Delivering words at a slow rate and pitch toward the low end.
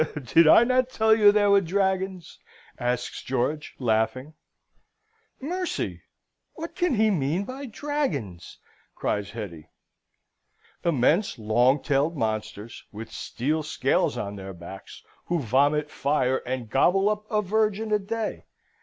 No: slow, 130 wpm; medium, 155 Hz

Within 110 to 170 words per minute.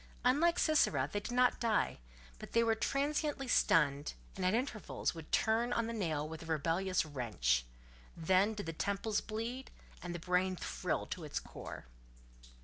Yes: average, 165 wpm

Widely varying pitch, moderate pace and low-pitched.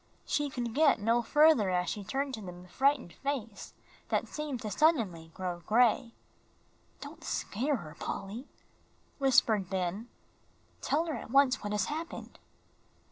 No: wide, 6.2 semitones; average, 145 wpm; high, 235 Hz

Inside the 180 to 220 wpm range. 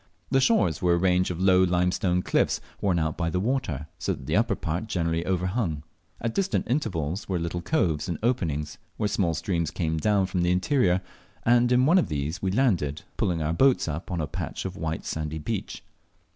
Yes: average, 200 wpm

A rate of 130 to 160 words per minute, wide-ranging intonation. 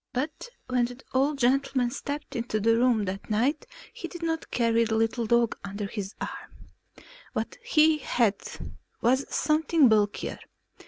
No: average, 150 wpm; average, 4.3 semitones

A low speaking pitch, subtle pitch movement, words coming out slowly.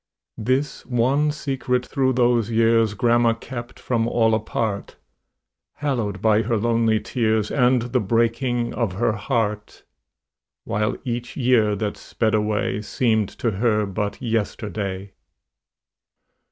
Yes: low, 115 Hz; narrow, 2.3 semitones; slow, 120 wpm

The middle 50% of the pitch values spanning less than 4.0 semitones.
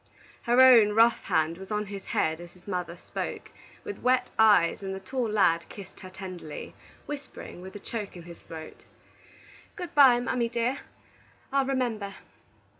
No: average, 5.3 semitones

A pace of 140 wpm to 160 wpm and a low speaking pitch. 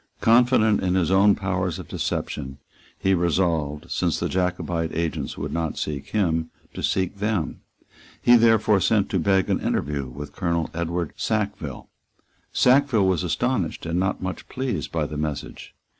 Yes: average, 155 wpm; very low, 90 Hz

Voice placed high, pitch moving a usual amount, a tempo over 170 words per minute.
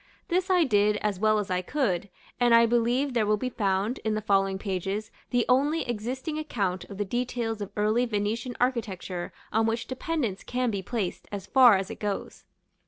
Yes: high, 220 Hz; average, 3.7 semitones; average, 190 wpm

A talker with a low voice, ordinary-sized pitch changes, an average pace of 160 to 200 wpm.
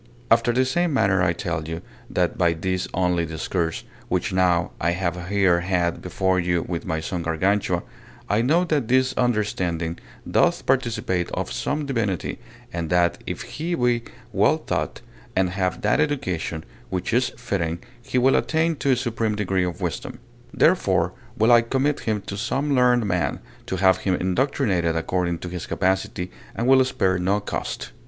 No: very low, 95 Hz; wide, 5.8 semitones; average, 170 wpm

